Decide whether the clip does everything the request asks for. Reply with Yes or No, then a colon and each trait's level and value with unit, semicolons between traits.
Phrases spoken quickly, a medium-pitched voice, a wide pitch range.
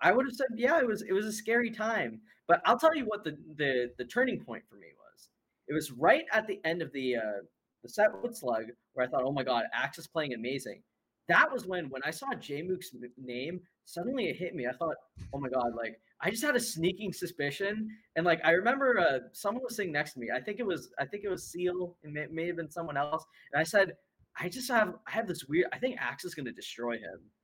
Yes: fast, 260 wpm; medium, 170 Hz; wide, 7.5 semitones